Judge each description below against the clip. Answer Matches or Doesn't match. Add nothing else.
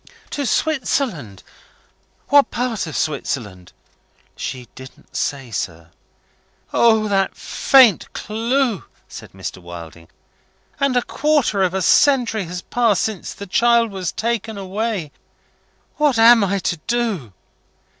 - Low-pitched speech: Doesn't match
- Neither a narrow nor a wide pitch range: Doesn't match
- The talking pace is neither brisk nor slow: Doesn't match